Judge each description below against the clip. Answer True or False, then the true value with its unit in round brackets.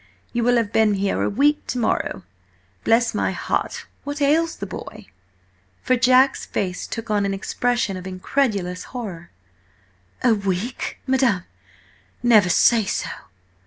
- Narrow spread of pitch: False (4.4 semitones)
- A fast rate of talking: False (140 wpm)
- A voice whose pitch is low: False (230 Hz)